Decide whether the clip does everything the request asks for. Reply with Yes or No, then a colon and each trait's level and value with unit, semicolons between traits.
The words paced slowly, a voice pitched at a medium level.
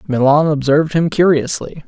Yes: slow, 130 wpm; medium, 150 Hz